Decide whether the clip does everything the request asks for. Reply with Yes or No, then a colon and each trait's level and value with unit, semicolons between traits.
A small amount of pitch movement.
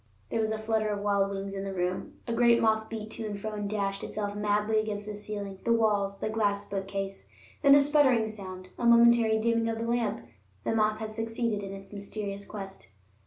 Yes: narrow, 2.0 semitones